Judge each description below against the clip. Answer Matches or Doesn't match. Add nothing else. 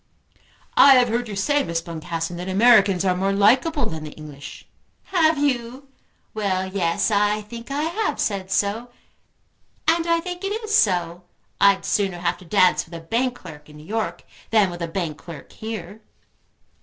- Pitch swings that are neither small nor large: Doesn't match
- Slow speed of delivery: Doesn't match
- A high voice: Matches